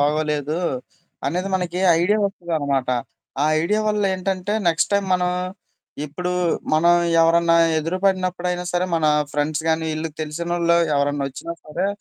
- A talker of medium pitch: Yes, medium, 170 Hz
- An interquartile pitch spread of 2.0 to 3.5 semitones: Yes, average, 2.8 semitones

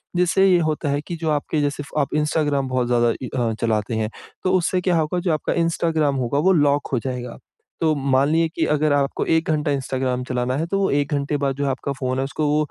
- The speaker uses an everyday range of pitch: Yes, average, 3.2 semitones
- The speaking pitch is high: No, medium, 145 Hz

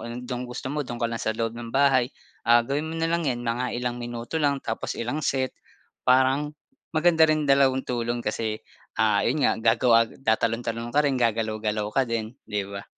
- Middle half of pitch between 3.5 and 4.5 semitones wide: No, average, 3.0 semitones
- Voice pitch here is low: Yes, low, 120 Hz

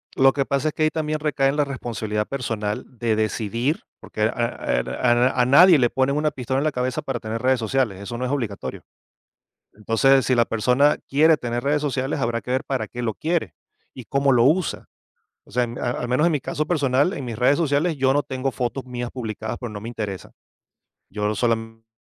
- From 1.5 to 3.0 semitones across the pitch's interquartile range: No, average, 3.4 semitones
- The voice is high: No, low, 125 Hz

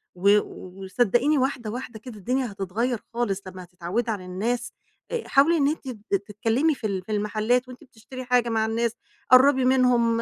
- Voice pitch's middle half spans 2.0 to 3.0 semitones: No, average, 3.7 semitones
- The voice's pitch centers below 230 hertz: No, high, 235 Hz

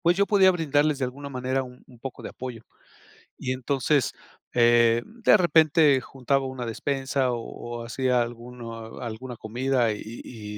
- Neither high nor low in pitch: No, low, 130 Hz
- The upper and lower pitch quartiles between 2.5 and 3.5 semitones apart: Yes, average, 2.9 semitones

